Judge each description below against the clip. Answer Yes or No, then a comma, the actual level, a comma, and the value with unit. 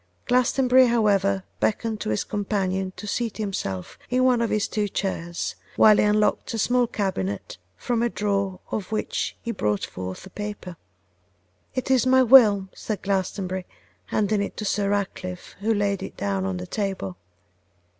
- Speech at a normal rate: Yes, average, 165 wpm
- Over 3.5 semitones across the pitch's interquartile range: No, average, 3.2 semitones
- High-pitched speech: Yes, high, 205 Hz